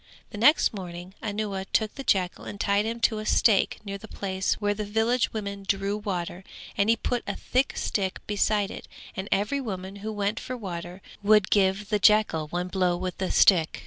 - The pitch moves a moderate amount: No, narrow, 2.2 semitones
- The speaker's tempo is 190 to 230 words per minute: Yes, average, 200 wpm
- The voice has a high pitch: Yes, high, 200 Hz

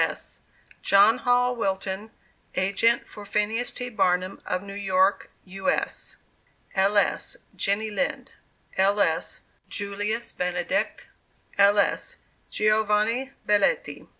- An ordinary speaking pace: No, slow, 110 wpm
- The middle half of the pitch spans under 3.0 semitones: Yes, narrow, 2.5 semitones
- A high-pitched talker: Yes, high, 205 Hz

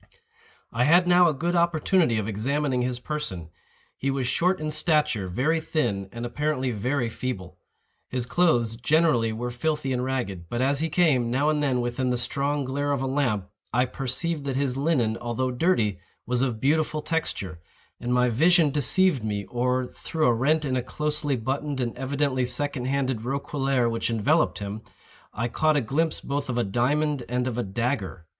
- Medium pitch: No, low, 130 Hz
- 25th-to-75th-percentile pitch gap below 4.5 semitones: Yes, average, 4.0 semitones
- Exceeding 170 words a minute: Yes, average, 180 wpm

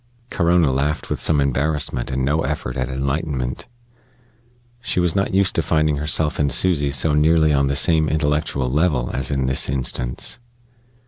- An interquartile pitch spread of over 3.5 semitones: No, average, 3.0 semitones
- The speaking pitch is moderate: No, very low, 75 Hz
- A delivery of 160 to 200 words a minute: Yes, average, 165 wpm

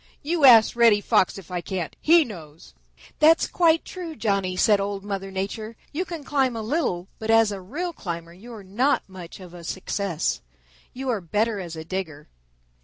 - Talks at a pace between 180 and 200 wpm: Yes, average, 185 wpm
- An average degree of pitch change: No, wide, 5.8 semitones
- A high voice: Yes, high, 205 Hz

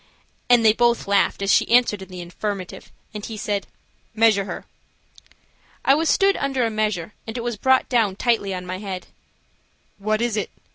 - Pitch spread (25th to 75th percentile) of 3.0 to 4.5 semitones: Yes, average, 3.3 semitones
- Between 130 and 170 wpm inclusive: No, average, 185 wpm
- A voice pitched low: No, high, 215 Hz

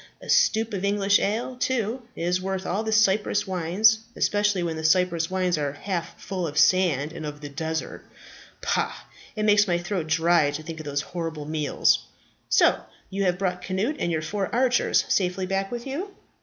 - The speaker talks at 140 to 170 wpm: No, average, 185 wpm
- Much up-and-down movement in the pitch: No, average, 4.2 semitones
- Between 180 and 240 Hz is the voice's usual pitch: Yes, medium, 185 Hz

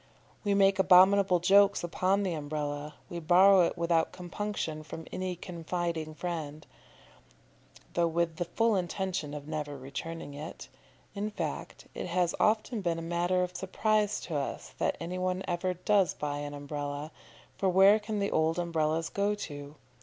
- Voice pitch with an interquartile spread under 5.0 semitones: Yes, average, 3.6 semitones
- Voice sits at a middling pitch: Yes, medium, 175 Hz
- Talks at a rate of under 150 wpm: No, average, 160 wpm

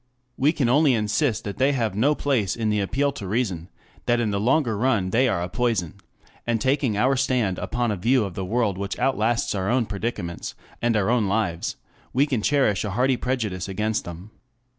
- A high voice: No, low, 115 Hz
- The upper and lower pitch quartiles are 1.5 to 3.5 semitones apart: No, average, 4.3 semitones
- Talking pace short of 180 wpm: No, fast, 205 wpm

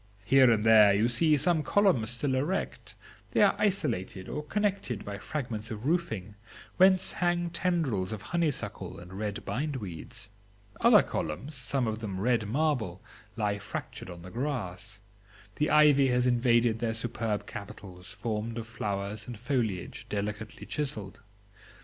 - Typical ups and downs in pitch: No, wide, 5.8 semitones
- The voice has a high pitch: No, low, 115 Hz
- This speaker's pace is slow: No, average, 145 wpm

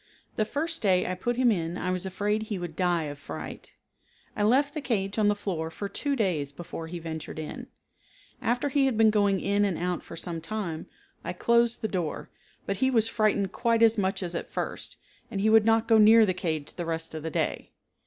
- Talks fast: Yes, fast, 220 wpm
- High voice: Yes, high, 200 Hz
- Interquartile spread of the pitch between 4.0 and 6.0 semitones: Yes, average, 4.5 semitones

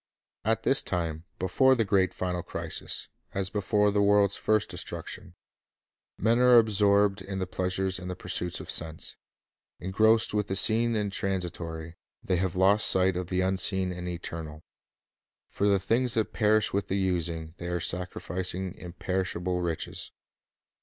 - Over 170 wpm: No, average, 155 wpm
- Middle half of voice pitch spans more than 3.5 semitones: No, narrow, 2.6 semitones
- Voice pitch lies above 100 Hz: No, very low, 95 Hz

